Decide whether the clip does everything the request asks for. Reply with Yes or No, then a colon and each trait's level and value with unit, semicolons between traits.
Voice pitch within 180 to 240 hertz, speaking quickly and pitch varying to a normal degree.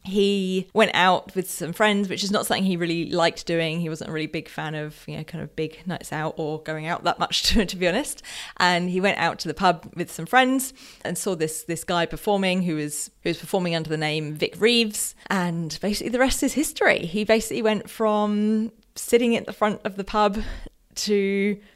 Yes: medium, 185 Hz; fast, 225 wpm; average, 4.3 semitones